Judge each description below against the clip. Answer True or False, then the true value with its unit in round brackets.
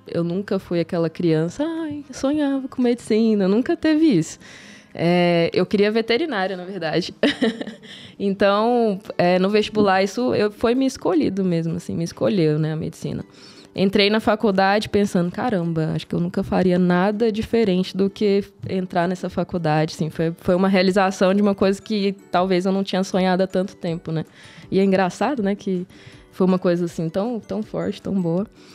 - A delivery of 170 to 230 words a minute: True (175 wpm)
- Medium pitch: False (195 Hz)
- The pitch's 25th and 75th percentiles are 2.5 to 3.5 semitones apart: True (3.1 semitones)